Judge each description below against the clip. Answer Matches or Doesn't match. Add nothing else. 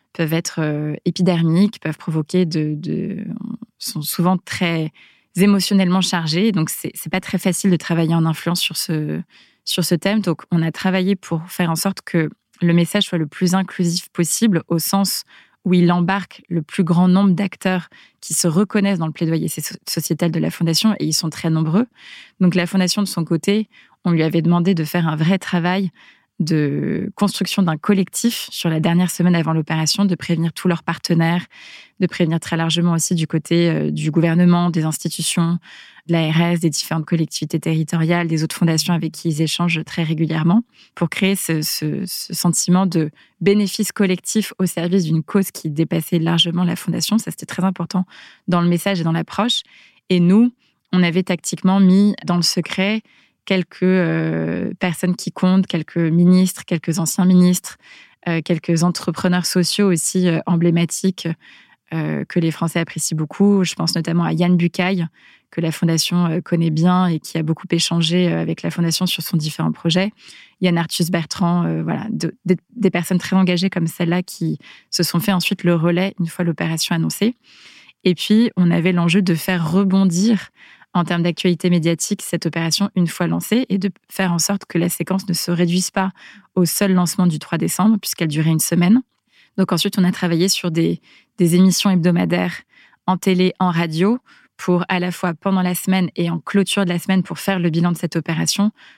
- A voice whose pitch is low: Doesn't match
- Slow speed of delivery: Doesn't match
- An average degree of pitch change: Doesn't match